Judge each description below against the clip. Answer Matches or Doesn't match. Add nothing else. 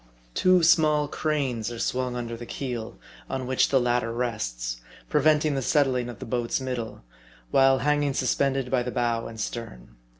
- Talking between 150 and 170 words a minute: Matches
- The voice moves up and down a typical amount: Matches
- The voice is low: Matches